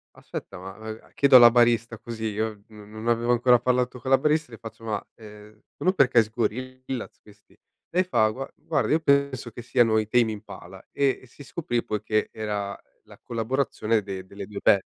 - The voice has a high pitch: No, low, 115 Hz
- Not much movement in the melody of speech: No, average, 3.0 semitones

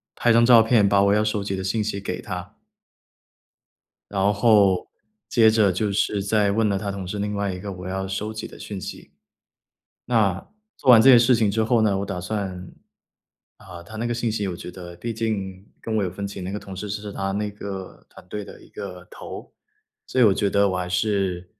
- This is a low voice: Yes, low, 100 Hz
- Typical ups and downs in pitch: No, narrow, 2.2 semitones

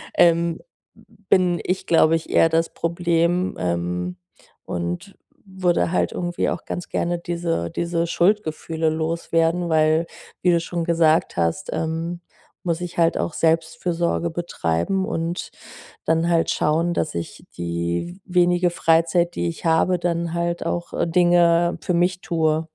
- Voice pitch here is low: No, medium, 170 Hz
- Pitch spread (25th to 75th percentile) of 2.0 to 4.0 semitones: No, narrow, 1.3 semitones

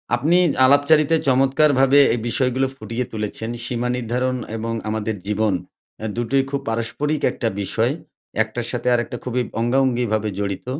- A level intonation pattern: No, average, 3.2 semitones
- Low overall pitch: Yes, low, 125 Hz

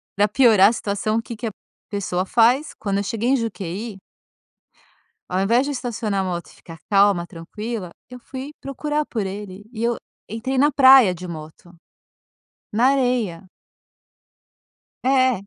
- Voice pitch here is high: Yes, high, 220 Hz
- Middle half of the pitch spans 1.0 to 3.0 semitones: No, average, 4.6 semitones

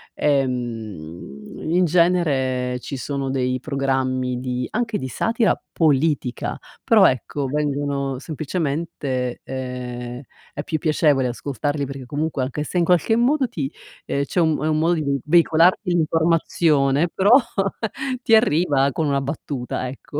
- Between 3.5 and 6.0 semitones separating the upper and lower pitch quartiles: Yes, average, 4.0 semitones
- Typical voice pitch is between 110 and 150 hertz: Yes, medium, 140 Hz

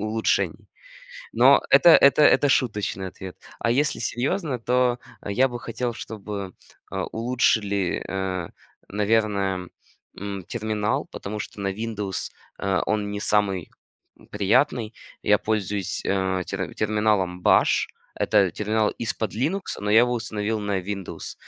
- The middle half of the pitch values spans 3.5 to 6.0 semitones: No, average, 2.7 semitones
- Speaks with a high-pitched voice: No, low, 105 Hz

